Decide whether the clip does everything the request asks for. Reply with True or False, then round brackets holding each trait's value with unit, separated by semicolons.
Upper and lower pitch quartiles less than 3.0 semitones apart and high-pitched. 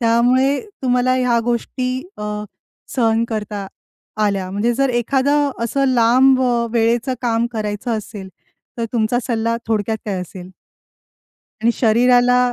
True (2.4 semitones; 235 Hz)